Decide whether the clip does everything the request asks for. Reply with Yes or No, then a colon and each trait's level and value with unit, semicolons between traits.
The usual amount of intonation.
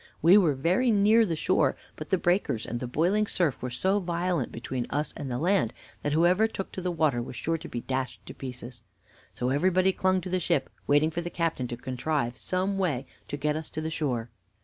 No: wide, 6.1 semitones